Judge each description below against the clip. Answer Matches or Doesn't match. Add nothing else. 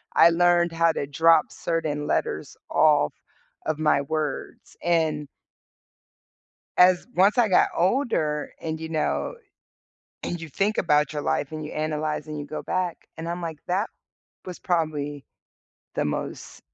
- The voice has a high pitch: Doesn't match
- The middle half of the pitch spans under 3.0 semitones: Matches